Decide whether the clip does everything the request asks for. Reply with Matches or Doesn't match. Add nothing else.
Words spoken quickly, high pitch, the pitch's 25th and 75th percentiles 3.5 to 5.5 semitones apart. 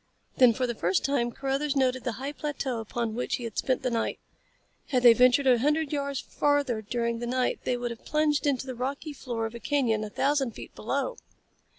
Doesn't match